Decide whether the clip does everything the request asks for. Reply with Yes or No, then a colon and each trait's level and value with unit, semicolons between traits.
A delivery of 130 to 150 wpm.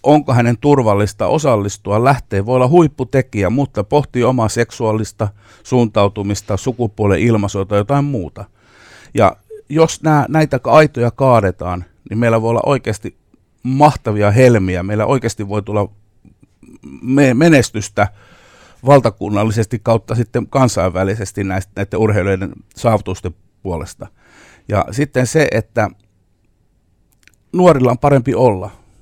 No: average, 110 wpm